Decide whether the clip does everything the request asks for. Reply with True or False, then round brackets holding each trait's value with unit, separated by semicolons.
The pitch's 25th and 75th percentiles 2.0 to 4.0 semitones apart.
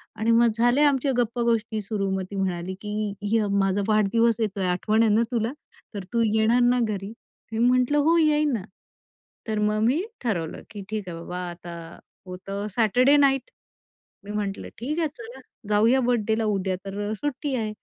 True (3.5 semitones)